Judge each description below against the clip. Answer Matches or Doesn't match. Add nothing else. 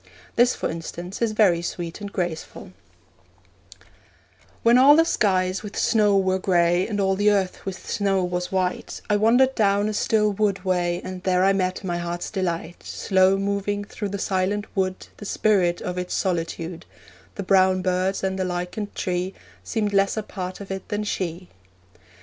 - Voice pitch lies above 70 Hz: Matches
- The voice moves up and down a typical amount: Doesn't match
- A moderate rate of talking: Matches